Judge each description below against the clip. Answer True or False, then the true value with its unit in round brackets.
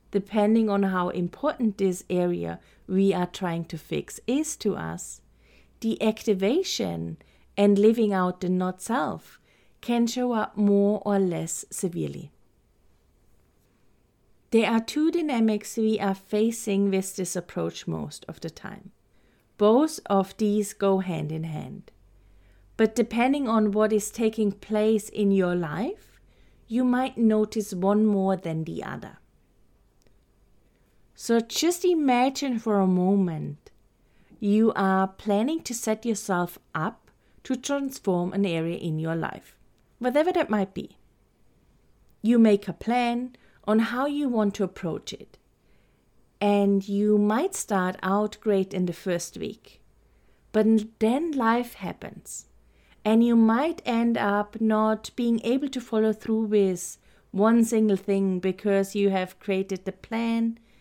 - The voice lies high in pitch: True (210 Hz)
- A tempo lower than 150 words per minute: True (135 wpm)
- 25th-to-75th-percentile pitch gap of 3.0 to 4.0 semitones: True (3.4 semitones)